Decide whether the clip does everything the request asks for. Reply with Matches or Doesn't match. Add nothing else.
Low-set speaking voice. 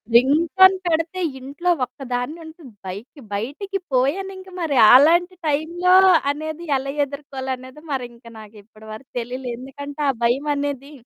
Doesn't match